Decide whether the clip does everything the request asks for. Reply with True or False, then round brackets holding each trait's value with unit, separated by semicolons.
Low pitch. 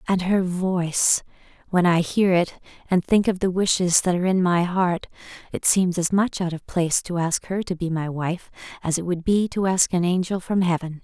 False (180 Hz)